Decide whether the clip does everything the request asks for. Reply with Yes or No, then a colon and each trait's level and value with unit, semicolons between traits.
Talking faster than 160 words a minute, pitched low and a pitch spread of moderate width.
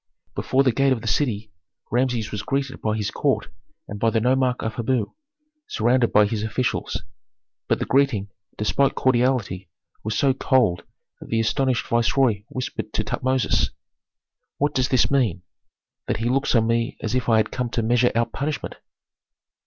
Yes: average, 170 wpm; low, 120 Hz; average, 3.1 semitones